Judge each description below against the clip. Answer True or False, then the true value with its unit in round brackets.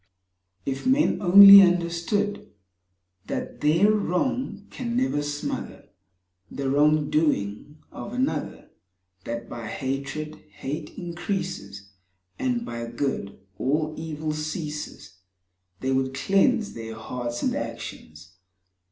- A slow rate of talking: True (105 wpm)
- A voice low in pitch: False (155 Hz)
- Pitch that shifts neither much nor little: False (6.8 semitones)